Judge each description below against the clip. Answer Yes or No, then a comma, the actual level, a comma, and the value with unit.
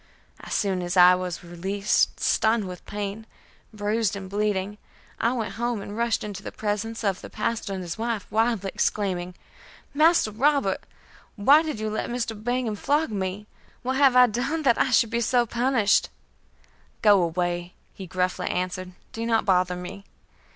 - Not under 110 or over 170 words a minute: Yes, average, 165 wpm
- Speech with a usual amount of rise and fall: Yes, average, 3.9 semitones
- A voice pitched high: Yes, high, 210 Hz